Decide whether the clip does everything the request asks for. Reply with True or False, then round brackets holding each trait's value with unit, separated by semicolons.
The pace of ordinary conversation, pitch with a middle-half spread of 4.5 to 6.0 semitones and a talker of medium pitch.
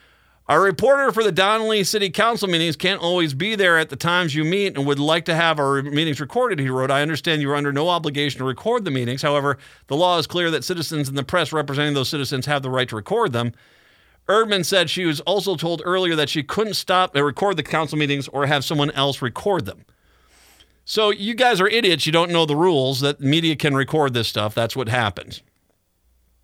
False (220 wpm; 4.8 semitones; 155 Hz)